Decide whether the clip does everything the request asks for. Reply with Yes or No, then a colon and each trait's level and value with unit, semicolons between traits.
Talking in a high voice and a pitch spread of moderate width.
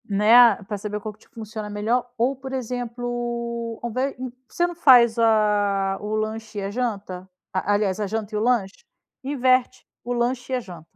Yes: high, 225 Hz; average, 3.0 semitones